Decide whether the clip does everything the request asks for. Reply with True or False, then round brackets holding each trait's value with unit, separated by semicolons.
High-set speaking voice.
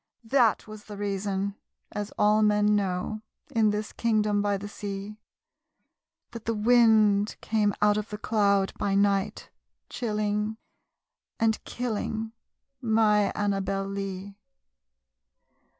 True (210 Hz)